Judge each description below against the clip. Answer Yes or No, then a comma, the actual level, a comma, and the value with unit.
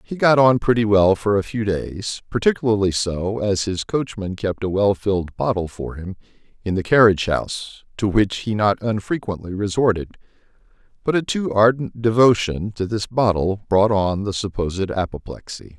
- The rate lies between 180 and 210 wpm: No, average, 165 wpm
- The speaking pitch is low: Yes, low, 105 Hz